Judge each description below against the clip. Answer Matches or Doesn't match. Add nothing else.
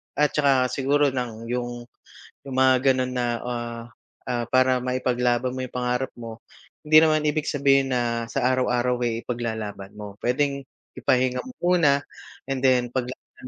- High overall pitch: Doesn't match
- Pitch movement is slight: Matches